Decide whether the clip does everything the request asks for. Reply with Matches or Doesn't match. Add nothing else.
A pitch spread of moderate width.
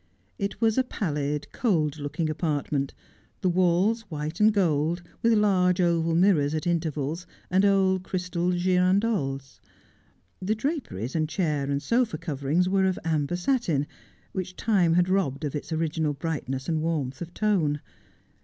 Matches